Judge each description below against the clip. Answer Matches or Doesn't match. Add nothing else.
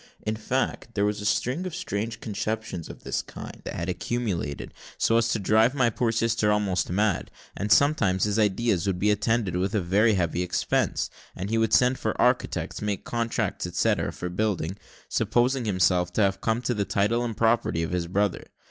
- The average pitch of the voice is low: Matches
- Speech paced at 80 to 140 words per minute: Doesn't match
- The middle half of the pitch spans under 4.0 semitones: Matches